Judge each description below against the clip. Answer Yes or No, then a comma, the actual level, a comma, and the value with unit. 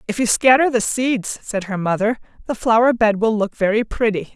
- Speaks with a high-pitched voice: Yes, high, 220 Hz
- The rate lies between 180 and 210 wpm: Yes, fast, 205 wpm